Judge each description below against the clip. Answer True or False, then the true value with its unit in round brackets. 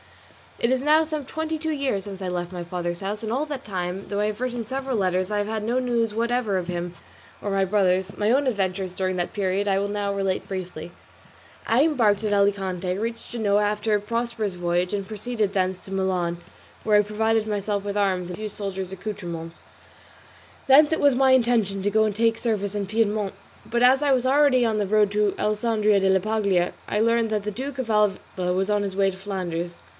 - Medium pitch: False (205 Hz)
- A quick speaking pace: True (220 wpm)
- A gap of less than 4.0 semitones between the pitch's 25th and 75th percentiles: True (3.3 semitones)